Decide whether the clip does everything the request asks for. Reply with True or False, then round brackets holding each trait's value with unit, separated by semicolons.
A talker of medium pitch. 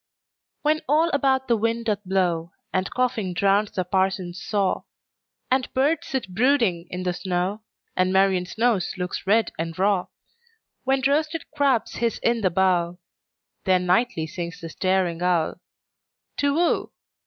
False (195 Hz)